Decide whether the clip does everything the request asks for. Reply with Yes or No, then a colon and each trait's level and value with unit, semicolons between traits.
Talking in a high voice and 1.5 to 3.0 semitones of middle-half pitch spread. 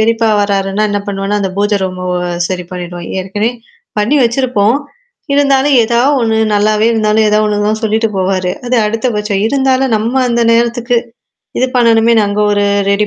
Yes: high, 215 Hz; average, 2.7 semitones